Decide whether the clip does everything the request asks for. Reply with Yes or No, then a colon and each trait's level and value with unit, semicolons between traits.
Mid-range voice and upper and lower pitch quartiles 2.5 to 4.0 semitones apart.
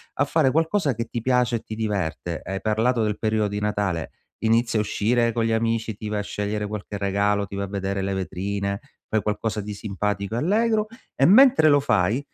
No: low, 105 Hz; average, 2.8 semitones